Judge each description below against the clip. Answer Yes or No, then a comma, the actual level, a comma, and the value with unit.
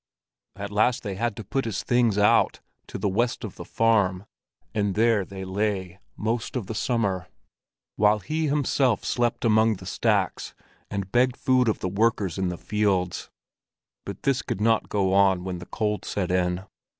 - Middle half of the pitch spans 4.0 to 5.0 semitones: No, average, 3.5 semitones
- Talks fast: No, average, 175 wpm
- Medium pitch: No, low, 105 Hz